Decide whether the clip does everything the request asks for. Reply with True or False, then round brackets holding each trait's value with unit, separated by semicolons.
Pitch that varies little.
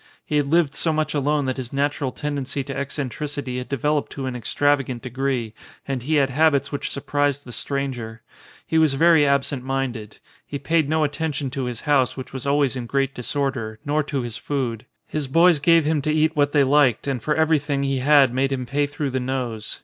True (2.2 semitones)